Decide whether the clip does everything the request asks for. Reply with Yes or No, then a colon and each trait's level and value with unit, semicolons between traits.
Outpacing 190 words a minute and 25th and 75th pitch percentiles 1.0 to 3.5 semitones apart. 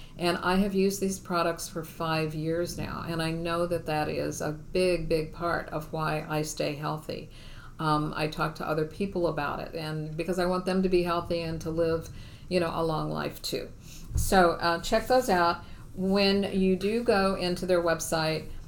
Yes: average, 200 wpm; average, 2.7 semitones